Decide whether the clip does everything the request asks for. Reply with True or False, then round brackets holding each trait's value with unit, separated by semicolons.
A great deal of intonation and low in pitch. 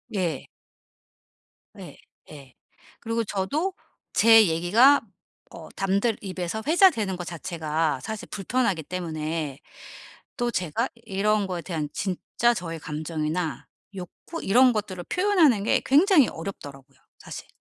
False (6.1 semitones; 190 Hz)